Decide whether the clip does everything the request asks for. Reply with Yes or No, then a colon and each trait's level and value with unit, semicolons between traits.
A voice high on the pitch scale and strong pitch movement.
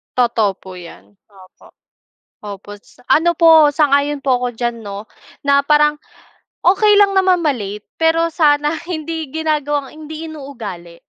Yes: very high, 290 Hz; wide, 6.1 semitones